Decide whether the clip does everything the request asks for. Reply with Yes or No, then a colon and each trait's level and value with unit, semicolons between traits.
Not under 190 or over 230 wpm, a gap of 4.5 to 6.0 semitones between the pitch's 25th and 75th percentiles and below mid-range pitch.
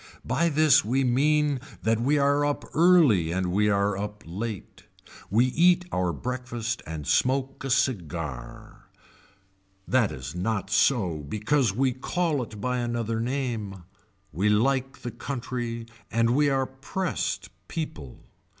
No: slow, 135 wpm; average, 5.2 semitones; low, 120 Hz